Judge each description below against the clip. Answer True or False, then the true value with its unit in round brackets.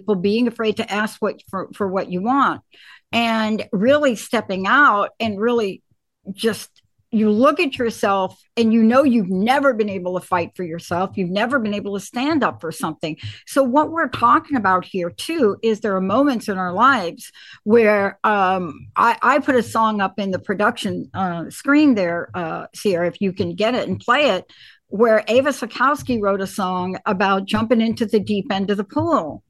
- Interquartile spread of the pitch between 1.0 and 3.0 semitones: False (3.9 semitones)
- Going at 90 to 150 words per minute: False (195 wpm)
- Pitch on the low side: False (215 Hz)